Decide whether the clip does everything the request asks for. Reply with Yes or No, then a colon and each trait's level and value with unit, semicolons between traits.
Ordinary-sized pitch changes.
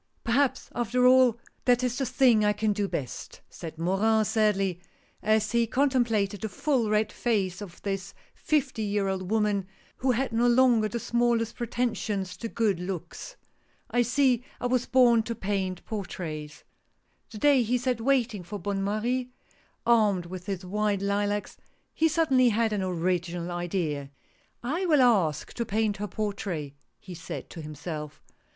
Yes: average, 4.2 semitones